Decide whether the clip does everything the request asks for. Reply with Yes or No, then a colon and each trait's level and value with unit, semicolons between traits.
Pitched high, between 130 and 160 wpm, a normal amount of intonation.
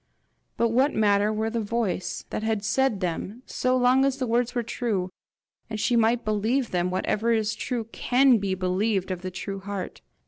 No: high, 220 Hz; average, 185 wpm; average, 3.6 semitones